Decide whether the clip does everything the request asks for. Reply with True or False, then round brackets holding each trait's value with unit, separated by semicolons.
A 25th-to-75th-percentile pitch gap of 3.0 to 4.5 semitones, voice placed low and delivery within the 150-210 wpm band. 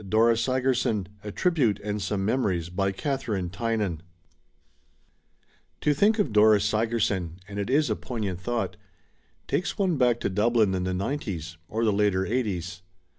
True (4.0 semitones; 105 Hz; 160 wpm)